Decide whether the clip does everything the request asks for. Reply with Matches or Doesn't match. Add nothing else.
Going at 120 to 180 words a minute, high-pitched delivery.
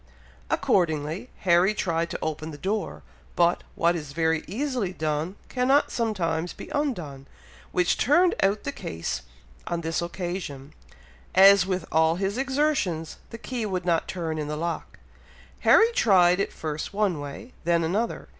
Doesn't match